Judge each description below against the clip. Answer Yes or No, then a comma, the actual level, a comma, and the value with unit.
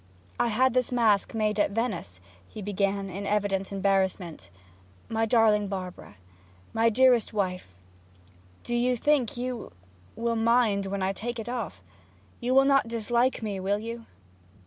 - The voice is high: Yes, high, 220 Hz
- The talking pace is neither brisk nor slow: Yes, average, 145 wpm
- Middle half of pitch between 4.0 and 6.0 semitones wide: No, average, 3.3 semitones